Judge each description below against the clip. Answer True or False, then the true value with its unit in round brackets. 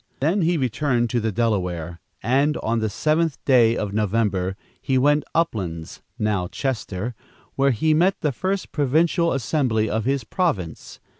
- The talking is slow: False (155 wpm)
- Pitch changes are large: True (6.1 semitones)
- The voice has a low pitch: True (120 Hz)